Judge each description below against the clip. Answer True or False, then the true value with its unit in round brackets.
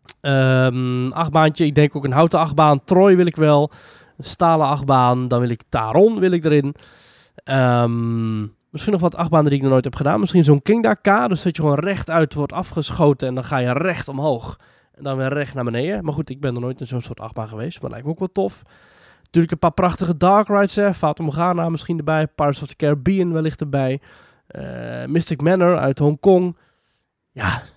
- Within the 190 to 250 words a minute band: True (200 wpm)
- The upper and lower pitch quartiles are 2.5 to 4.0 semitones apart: False (4.6 semitones)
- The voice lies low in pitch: False (150 Hz)